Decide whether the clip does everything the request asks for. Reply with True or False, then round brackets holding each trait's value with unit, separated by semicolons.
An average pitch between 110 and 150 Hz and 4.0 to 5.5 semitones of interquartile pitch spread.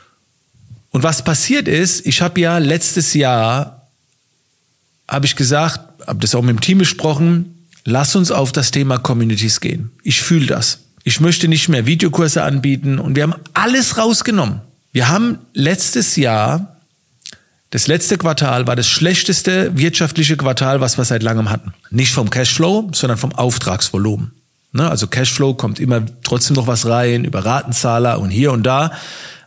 True (140 Hz; 5.1 semitones)